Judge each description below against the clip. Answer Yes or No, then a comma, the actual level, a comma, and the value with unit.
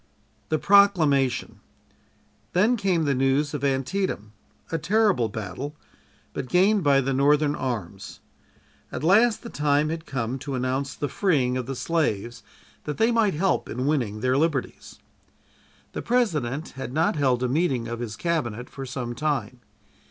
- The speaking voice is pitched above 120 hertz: Yes, medium, 140 Hz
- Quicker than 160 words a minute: No, average, 150 wpm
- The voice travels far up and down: No, average, 4.8 semitones